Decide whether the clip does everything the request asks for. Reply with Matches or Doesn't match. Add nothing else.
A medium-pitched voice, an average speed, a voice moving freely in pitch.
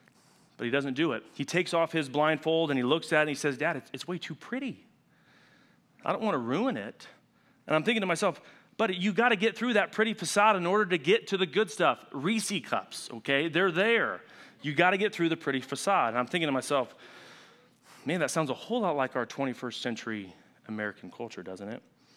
Doesn't match